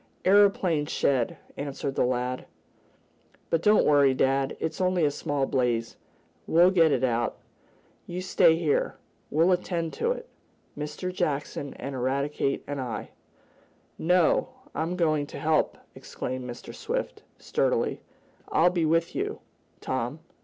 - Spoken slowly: Yes, slow, 130 wpm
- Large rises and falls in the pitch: No, average, 4.2 semitones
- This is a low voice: No, medium, 150 Hz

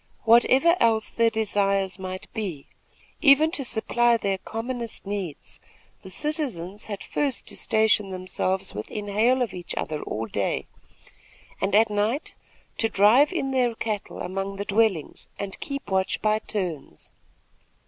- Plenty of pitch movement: No, average, 3.8 semitones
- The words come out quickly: No, average, 140 wpm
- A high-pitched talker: Yes, high, 210 Hz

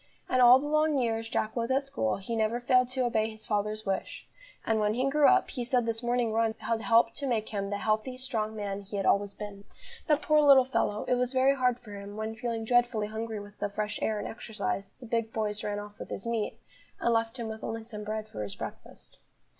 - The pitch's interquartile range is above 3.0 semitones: No, average, 2.7 semitones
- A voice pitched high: Yes, high, 225 Hz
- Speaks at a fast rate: Yes, fast, 240 wpm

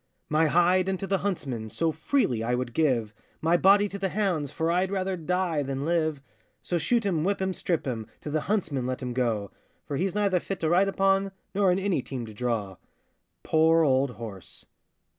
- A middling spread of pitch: No, wide, 6.6 semitones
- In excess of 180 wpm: Yes, average, 200 wpm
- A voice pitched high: No, medium, 165 Hz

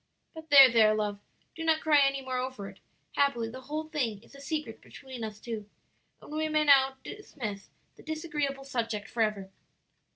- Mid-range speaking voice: No, very high, 265 Hz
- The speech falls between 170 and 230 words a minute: Yes, average, 175 wpm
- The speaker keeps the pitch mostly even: No, average, 5.3 semitones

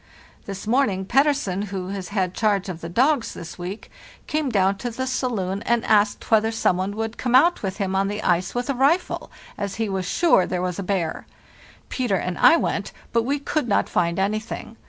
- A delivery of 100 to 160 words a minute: No, fast, 205 wpm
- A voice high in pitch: Yes, high, 205 Hz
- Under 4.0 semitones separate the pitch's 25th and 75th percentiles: No, average, 4.5 semitones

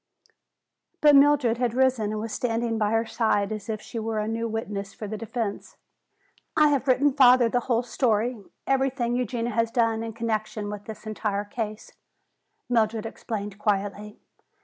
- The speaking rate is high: No, average, 165 wpm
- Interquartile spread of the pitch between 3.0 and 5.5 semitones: No, narrow, 2.4 semitones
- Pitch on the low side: No, high, 225 Hz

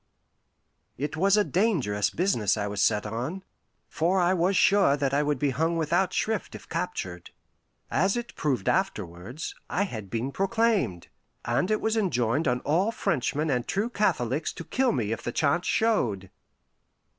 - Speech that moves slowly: No, average, 165 wpm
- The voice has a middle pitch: Yes, medium, 155 Hz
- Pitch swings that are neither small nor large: No, wide, 8.4 semitones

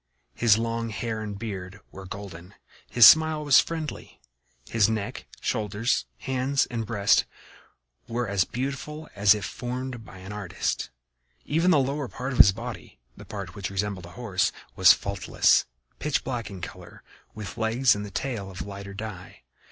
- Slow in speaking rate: No, average, 160 wpm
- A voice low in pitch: Yes, low, 110 Hz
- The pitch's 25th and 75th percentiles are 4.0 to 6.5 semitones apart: Yes, average, 4.3 semitones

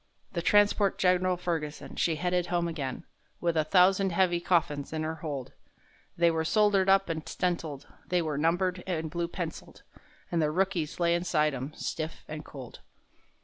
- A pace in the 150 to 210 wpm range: Yes, average, 165 wpm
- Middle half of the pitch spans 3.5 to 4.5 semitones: No, narrow, 2.6 semitones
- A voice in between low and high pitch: Yes, medium, 170 Hz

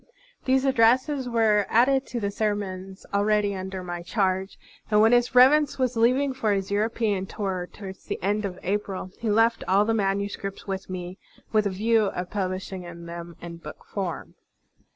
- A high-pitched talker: Yes, high, 205 Hz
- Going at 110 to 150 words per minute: No, average, 175 wpm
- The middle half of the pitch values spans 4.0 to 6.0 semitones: No, average, 3.2 semitones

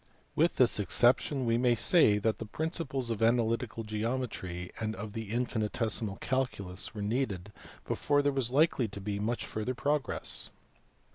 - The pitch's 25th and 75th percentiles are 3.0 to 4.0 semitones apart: Yes, average, 3.6 semitones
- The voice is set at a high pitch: No, low, 115 Hz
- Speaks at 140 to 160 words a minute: Yes, average, 150 wpm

